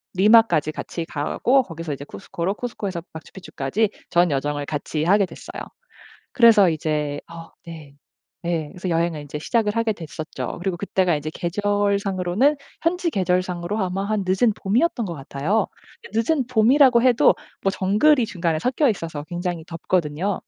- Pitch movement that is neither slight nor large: Yes, average, 5.0 semitones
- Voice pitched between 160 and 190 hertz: Yes, medium, 185 Hz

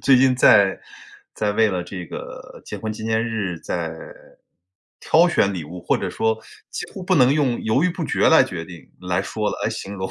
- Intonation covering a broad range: Yes, wide, 5.7 semitones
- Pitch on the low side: Yes, low, 110 Hz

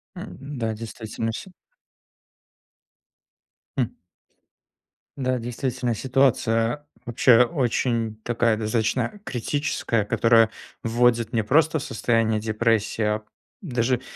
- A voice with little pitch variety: Yes, narrow, 2.1 semitones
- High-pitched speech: No, low, 115 Hz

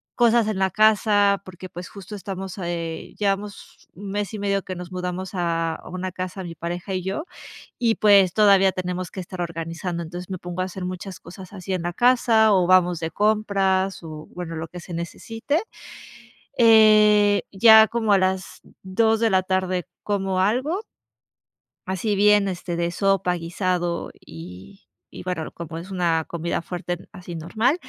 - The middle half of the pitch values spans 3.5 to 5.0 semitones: No, average, 2.8 semitones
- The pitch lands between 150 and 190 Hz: Yes, medium, 185 Hz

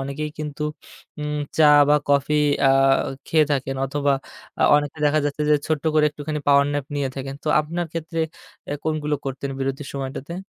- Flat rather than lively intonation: Yes, narrow, 1.7 semitones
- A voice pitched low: No, medium, 145 Hz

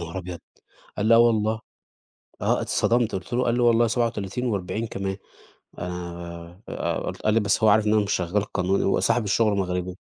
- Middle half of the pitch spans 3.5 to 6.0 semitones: Yes, average, 3.9 semitones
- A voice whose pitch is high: No, low, 105 Hz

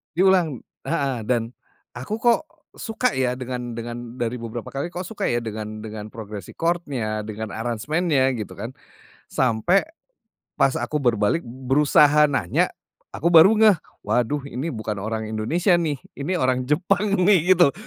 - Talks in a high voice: No, low, 130 Hz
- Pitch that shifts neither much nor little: No, wide, 6.6 semitones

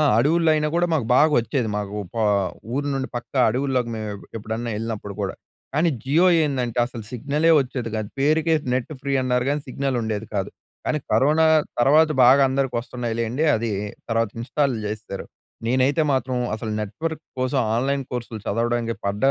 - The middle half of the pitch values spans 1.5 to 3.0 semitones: No, average, 3.8 semitones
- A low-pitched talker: Yes, low, 125 Hz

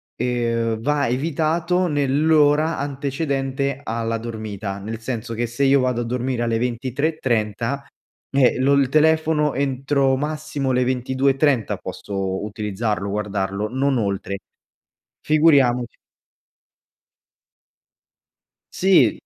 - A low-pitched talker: Yes, low, 130 Hz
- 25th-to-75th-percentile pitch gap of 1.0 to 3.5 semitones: No, average, 3.9 semitones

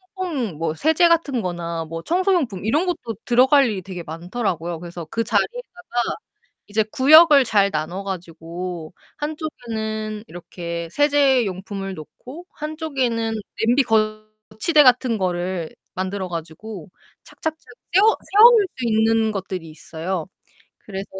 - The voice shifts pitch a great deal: Yes, wide, 7.8 semitones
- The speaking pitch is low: No, high, 215 Hz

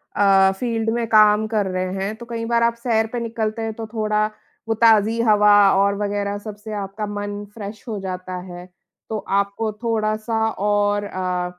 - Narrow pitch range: Yes, narrow, 1.9 semitones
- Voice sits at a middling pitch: No, high, 215 Hz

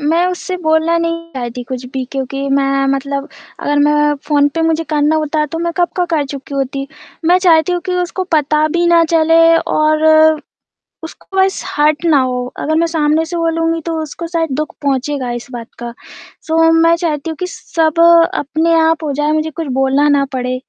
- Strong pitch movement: No, average, 2.9 semitones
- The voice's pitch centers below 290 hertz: No, very high, 310 Hz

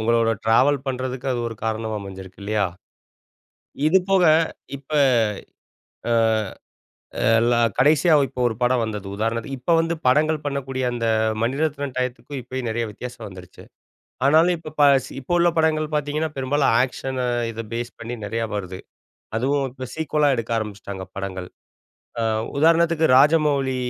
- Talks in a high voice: No, low, 130 Hz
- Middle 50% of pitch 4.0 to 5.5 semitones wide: Yes, average, 4.5 semitones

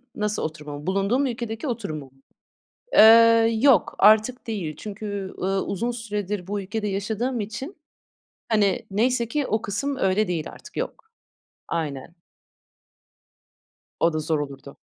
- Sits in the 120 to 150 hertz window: No, high, 210 Hz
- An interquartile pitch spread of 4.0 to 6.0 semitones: No, average, 3.6 semitones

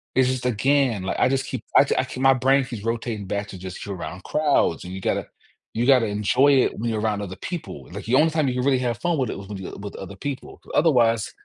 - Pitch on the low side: Yes, low, 120 Hz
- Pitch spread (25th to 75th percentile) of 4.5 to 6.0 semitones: Yes, average, 4.8 semitones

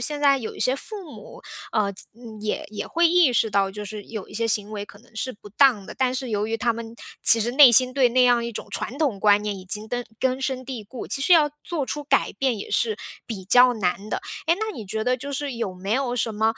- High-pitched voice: Yes, high, 235 Hz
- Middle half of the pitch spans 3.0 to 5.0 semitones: Yes, average, 4.0 semitones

